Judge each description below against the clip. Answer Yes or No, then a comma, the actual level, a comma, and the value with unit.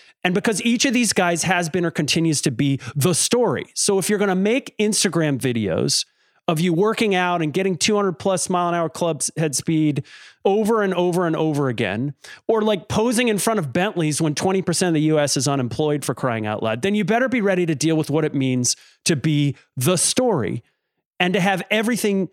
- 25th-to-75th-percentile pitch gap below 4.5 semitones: No, average, 5.2 semitones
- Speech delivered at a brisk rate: Yes, fast, 210 wpm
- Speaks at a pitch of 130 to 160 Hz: No, medium, 175 Hz